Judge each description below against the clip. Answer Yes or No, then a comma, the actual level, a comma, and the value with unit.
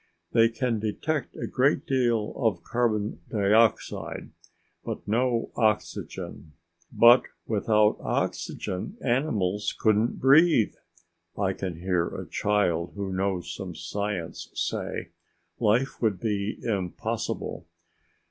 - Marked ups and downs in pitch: No, average, 3.3 semitones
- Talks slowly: Yes, slow, 105 wpm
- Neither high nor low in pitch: No, low, 105 Hz